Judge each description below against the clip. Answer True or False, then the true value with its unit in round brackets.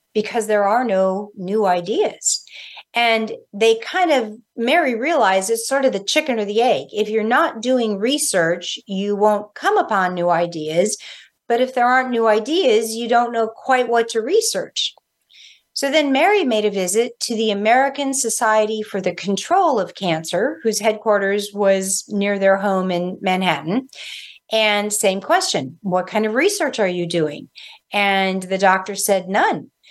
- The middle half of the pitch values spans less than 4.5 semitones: True (3.9 semitones)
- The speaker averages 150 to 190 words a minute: True (165 wpm)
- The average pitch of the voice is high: True (215 Hz)